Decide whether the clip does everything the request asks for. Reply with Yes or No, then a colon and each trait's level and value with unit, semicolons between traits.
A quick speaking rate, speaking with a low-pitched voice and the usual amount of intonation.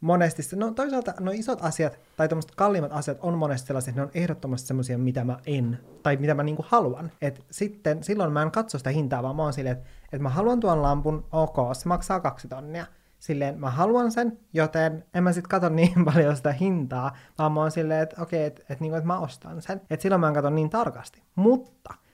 No: fast, 230 wpm; medium, 155 Hz; average, 3.9 semitones